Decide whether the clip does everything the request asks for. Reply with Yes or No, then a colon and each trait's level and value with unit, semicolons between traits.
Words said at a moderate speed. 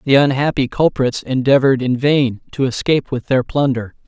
Yes: average, 160 wpm